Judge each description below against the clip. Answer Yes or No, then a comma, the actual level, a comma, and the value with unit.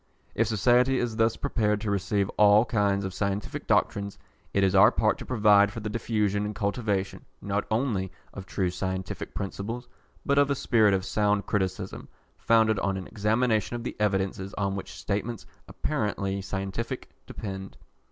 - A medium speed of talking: Yes, average, 160 wpm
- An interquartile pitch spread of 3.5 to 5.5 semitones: No, narrow, 2.5 semitones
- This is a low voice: Yes, low, 105 Hz